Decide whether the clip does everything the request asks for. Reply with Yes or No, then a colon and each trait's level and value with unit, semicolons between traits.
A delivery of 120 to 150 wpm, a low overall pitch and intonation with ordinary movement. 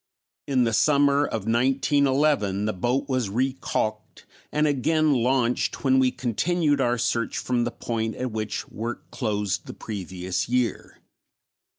Yes: average, 140 wpm; low, 125 Hz; average, 3.8 semitones